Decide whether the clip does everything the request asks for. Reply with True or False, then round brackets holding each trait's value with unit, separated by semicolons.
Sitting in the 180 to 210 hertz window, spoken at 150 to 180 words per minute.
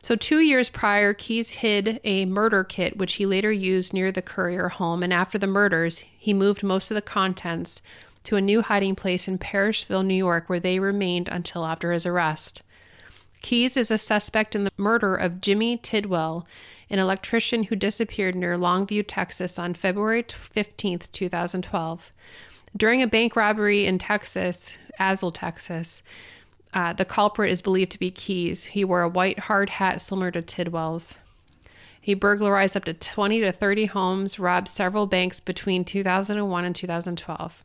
True (190 Hz; 165 wpm)